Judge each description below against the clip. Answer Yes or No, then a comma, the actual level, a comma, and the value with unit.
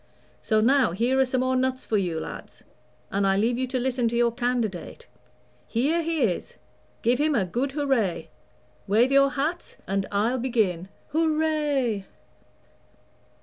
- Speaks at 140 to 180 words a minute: Yes, average, 150 wpm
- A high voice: Yes, high, 245 Hz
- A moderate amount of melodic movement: Yes, average, 4.3 semitones